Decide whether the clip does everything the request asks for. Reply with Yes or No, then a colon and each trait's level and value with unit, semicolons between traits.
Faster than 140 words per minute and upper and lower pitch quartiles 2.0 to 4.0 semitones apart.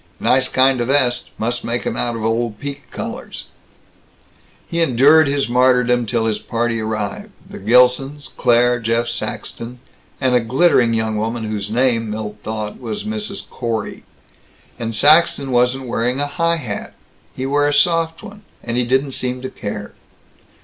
Yes: average, 160 wpm; average, 3.3 semitones